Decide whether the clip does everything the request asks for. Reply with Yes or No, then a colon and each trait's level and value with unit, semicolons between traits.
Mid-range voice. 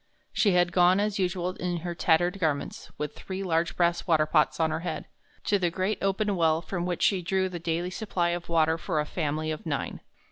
Yes: medium, 175 Hz